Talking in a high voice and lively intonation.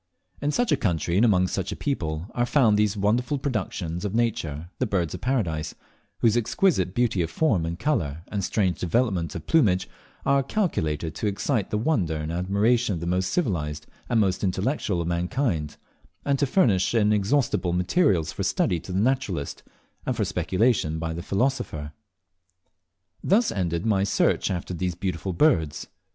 No: very low, 95 Hz; wide, 6.2 semitones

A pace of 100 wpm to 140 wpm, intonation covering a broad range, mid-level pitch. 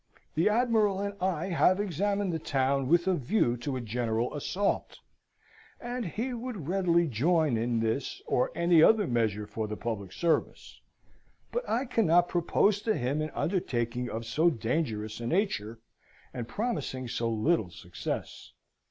No: average, 150 wpm; wide, 8.7 semitones; medium, 155 Hz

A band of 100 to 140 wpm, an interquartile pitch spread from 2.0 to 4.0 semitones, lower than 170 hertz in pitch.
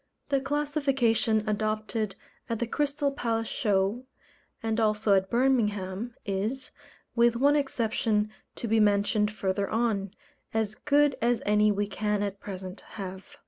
No: slow, 135 wpm; average, 3.0 semitones; high, 220 Hz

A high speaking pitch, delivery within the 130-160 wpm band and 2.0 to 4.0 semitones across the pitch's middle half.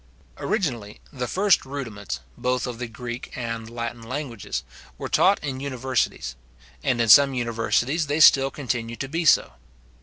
No: low, 125 Hz; average, 150 wpm; average, 3.3 semitones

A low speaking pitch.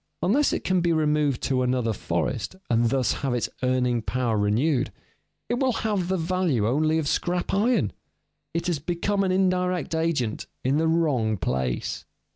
No: medium, 155 Hz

